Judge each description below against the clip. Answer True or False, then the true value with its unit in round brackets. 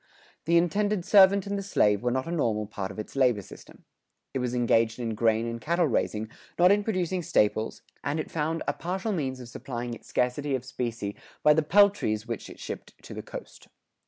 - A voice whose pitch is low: True (130 Hz)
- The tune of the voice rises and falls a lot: True (7.3 semitones)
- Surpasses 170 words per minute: True (205 wpm)